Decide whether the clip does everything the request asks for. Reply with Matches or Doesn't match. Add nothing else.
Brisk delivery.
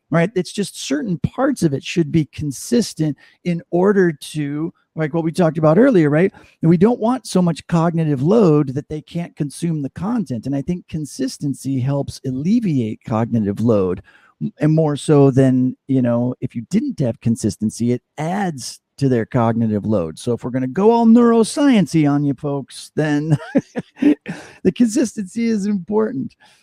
Doesn't match